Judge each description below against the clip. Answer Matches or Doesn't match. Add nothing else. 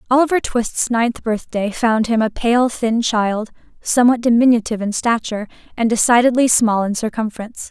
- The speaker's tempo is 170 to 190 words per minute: Doesn't match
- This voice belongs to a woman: Matches